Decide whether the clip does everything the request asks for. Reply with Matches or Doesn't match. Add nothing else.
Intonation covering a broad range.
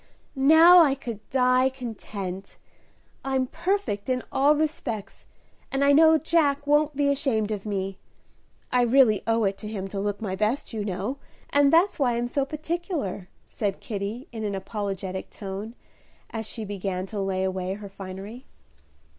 Matches